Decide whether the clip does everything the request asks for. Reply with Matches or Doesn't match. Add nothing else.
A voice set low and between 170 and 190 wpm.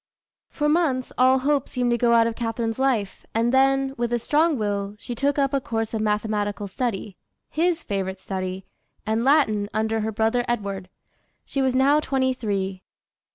Doesn't match